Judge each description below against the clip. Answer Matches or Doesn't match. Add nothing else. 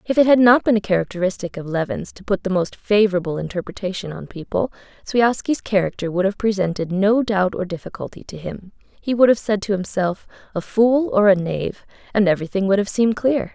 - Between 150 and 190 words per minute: Doesn't match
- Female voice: Matches